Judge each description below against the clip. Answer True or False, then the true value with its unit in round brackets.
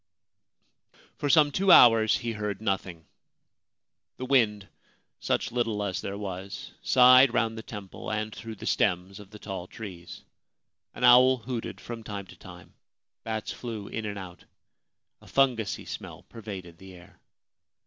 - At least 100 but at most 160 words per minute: True (155 wpm)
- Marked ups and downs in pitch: False (3.3 semitones)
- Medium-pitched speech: False (110 Hz)